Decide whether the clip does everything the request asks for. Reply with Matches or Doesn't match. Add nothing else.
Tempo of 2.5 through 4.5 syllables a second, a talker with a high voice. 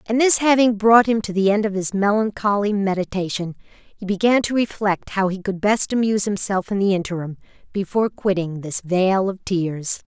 Doesn't match